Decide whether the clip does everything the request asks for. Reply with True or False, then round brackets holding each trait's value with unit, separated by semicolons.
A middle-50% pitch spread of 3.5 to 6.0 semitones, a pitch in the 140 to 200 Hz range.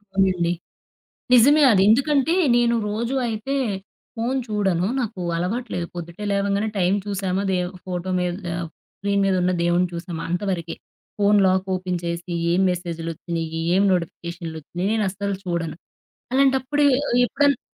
True (4.1 semitones; 190 Hz)